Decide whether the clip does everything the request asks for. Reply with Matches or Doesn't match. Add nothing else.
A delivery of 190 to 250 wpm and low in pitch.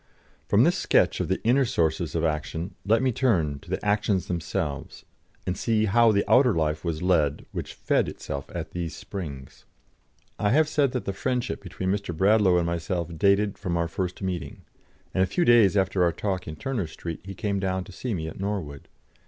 Matches